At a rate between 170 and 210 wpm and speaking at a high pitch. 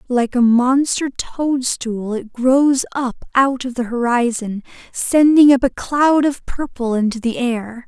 No: average, 150 wpm; very high, 255 Hz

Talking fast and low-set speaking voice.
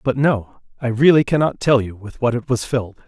Yes: fast, 215 wpm; low, 120 Hz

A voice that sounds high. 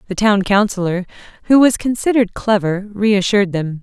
Yes: high, 205 Hz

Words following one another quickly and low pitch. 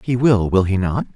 Yes: fast, 260 wpm; low, 105 Hz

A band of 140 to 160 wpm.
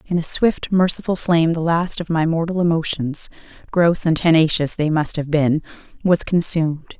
Yes: average, 155 wpm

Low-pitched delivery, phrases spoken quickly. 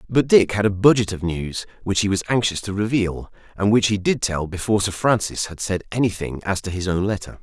Yes: low, 100 Hz; fast, 235 wpm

